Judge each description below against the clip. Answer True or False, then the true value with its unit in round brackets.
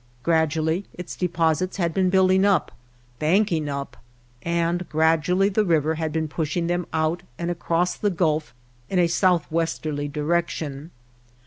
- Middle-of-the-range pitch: True (165 Hz)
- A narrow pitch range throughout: True (2.2 semitones)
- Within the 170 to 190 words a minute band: False (140 wpm)